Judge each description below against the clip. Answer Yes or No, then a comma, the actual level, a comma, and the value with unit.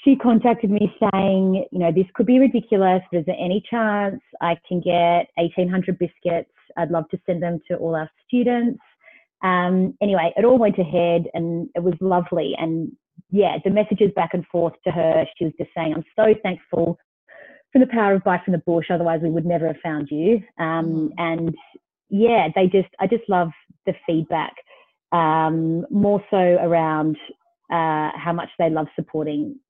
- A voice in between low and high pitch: Yes, medium, 180 Hz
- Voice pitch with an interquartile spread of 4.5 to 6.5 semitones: No, average, 3.5 semitones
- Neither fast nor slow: Yes, average, 180 wpm